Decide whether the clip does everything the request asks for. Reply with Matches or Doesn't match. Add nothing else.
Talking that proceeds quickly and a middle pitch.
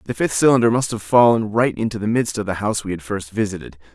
Doesn't match